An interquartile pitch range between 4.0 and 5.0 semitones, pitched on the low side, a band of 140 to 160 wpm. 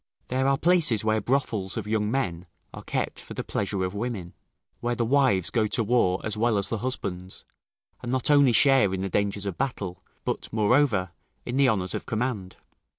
No: average, 4.7 semitones; low, 110 Hz; average, 195 wpm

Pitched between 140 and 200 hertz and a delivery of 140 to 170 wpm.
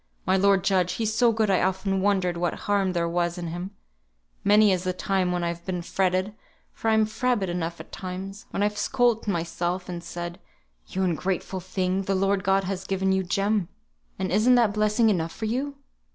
No: high, 190 Hz; average, 195 wpm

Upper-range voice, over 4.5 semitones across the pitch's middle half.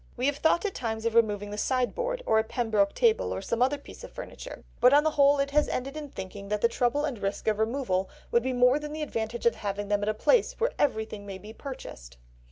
Yes: high, 240 Hz; wide, 5.4 semitones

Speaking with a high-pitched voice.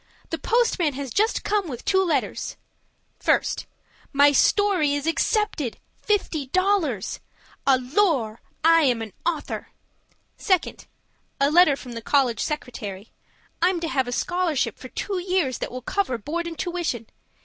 Yes: very high, 310 Hz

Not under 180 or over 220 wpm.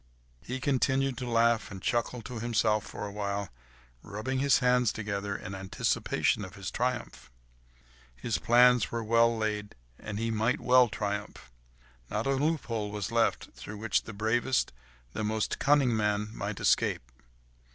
No: average, 150 wpm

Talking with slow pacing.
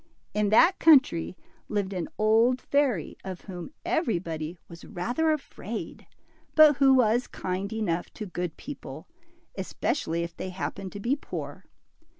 No: average, 145 wpm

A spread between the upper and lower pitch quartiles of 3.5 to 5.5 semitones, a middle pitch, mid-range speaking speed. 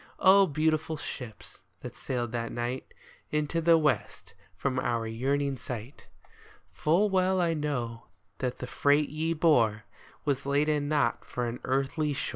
Yes: average, 4.1 semitones; medium, 145 Hz; average, 145 wpm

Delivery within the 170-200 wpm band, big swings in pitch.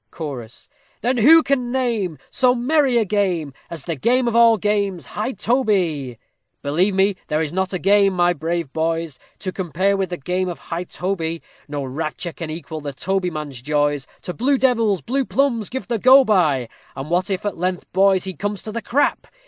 Yes: average, 190 wpm; wide, 5.7 semitones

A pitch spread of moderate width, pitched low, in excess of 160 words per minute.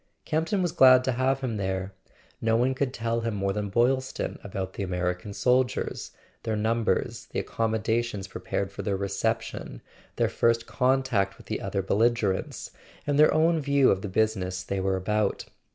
Yes: average, 4.7 semitones; low, 110 Hz; average, 170 wpm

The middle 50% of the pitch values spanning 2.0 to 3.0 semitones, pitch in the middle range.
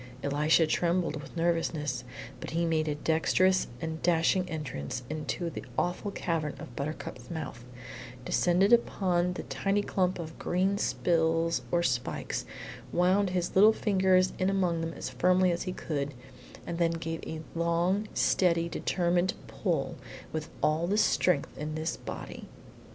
Yes: narrow, 2.5 semitones; medium, 170 Hz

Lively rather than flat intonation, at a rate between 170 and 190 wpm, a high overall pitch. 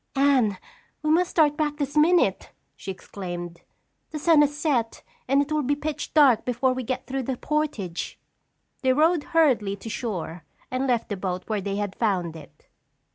Yes: wide, 6.8 semitones; average, 180 wpm; very high, 255 Hz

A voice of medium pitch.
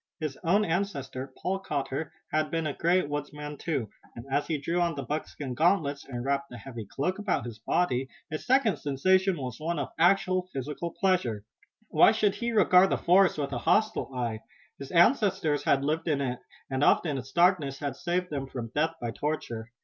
Yes: medium, 150 Hz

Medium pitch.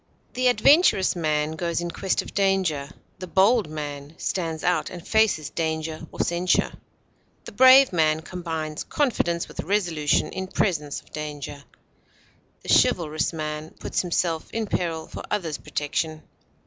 Yes: medium, 165 Hz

